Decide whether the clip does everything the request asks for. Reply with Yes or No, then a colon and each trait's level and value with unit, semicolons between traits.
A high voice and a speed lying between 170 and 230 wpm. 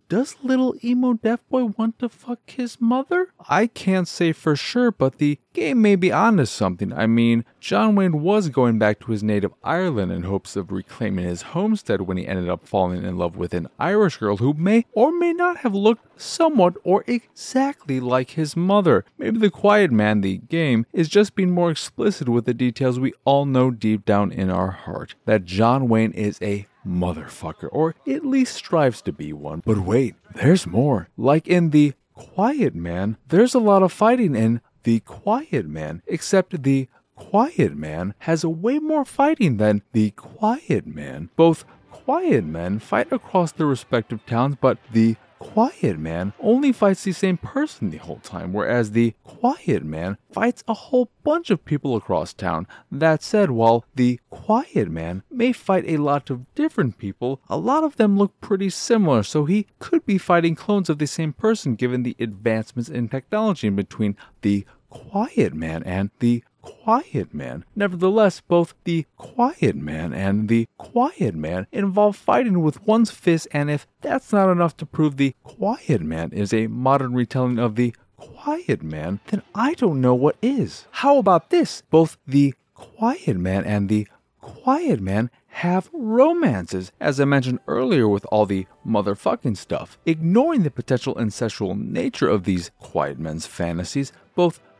No: medium, 145 Hz; average, 175 wpm